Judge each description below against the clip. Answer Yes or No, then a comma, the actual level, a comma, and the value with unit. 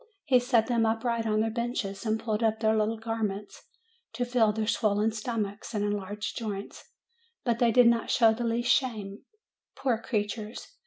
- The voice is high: Yes, high, 225 Hz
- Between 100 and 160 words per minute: No, average, 175 wpm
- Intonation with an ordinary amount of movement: No, narrow, 1.9 semitones